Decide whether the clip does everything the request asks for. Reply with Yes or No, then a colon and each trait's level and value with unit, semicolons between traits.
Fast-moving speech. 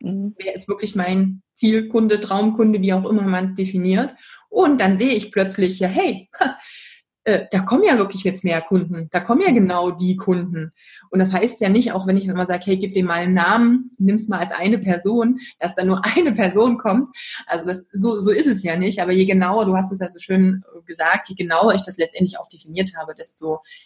Yes: fast, 220 wpm